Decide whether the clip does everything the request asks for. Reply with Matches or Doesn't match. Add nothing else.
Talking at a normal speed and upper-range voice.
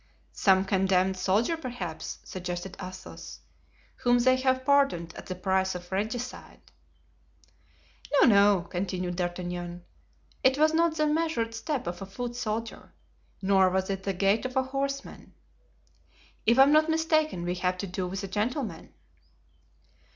Matches